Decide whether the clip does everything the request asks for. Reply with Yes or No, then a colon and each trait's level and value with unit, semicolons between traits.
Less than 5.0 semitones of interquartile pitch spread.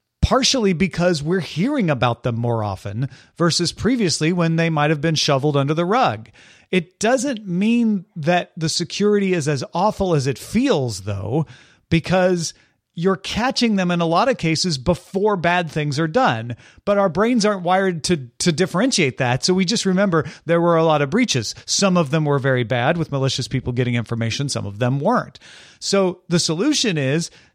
No: wide, 5.6 semitones